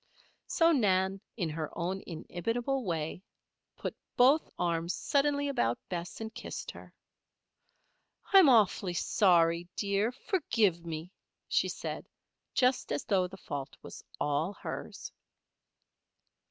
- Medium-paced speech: No, slow, 120 wpm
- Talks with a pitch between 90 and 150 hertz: No, high, 190 Hz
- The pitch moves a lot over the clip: Yes, wide, 6.4 semitones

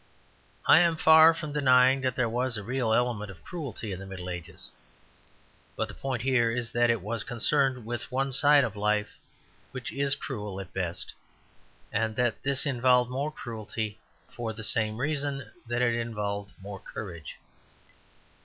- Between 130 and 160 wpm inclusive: No, average, 170 wpm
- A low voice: Yes, low, 120 Hz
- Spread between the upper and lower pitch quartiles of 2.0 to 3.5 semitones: No, average, 4.0 semitones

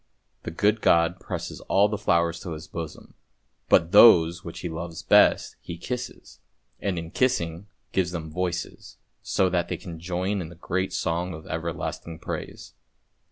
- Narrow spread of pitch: Yes, narrow, 2.1 semitones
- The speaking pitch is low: Yes, very low, 85 Hz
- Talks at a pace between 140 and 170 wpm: Yes, average, 165 wpm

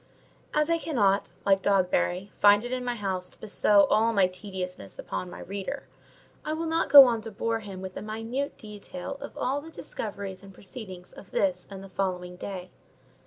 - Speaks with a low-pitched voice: No, high, 200 Hz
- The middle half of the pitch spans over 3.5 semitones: Yes, average, 4.4 semitones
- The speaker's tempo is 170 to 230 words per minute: Yes, average, 190 wpm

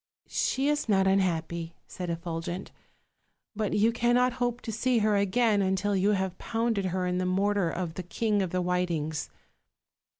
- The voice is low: No, high, 190 Hz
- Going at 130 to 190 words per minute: Yes, average, 170 wpm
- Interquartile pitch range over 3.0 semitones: Yes, average, 3.6 semitones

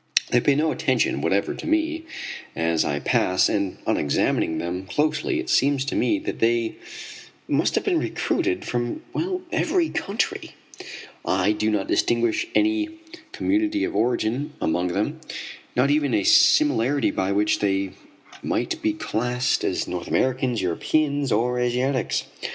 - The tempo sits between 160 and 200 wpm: No, average, 145 wpm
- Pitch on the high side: No, low, 125 Hz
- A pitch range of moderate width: No, wide, 7.0 semitones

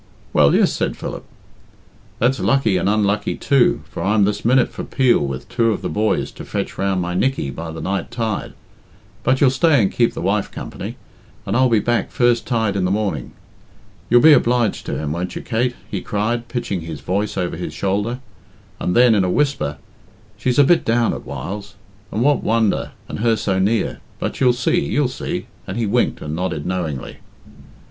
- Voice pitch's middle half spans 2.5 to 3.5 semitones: No, average, 4.6 semitones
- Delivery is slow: No, average, 195 wpm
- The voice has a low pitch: Yes, low, 110 Hz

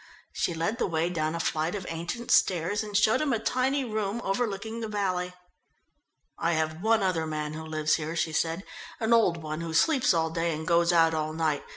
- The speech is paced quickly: Yes, fast, 210 wpm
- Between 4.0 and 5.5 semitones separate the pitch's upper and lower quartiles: Yes, average, 4.9 semitones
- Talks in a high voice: No, medium, 170 Hz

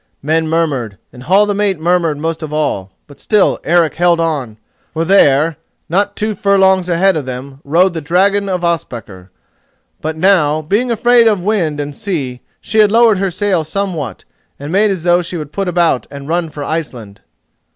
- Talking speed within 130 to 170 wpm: No, average, 185 wpm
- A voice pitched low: No, medium, 165 Hz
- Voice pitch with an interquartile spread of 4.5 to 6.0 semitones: Yes, average, 4.9 semitones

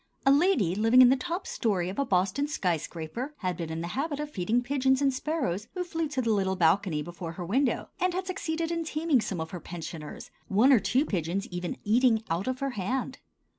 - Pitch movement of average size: No, wide, 7.9 semitones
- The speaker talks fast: Yes, fast, 220 wpm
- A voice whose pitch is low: No, high, 235 Hz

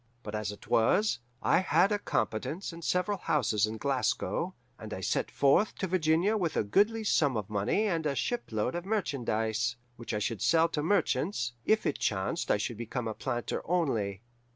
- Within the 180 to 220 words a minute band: Yes, average, 185 wpm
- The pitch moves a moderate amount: No, wide, 8.8 semitones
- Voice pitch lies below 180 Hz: Yes, medium, 140 Hz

